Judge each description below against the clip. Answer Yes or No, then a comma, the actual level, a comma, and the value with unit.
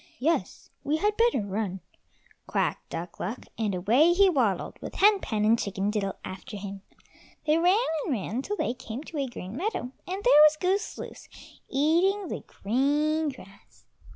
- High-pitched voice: Yes, very high, 270 Hz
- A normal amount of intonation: No, wide, 8.4 semitones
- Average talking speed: Yes, average, 170 wpm